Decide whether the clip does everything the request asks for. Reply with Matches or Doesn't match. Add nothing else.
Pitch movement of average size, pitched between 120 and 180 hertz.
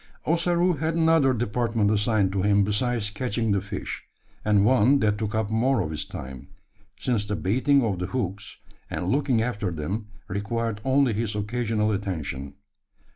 Doesn't match